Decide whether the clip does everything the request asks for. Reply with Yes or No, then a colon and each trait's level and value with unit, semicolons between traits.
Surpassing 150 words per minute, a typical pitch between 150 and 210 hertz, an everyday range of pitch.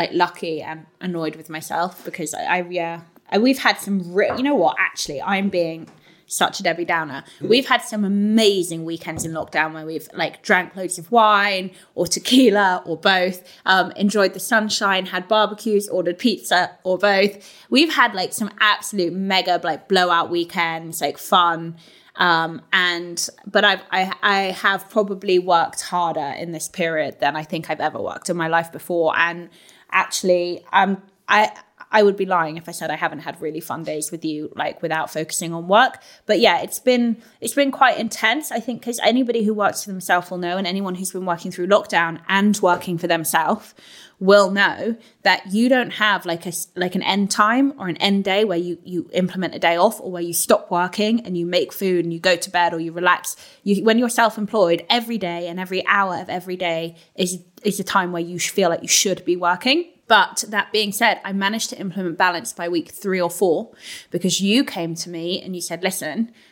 Yes: fast, 205 wpm; medium, 185 Hz; average, 3.3 semitones